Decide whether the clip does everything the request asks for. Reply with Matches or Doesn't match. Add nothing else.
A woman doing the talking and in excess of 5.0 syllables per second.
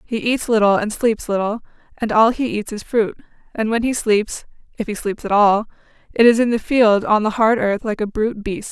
Matches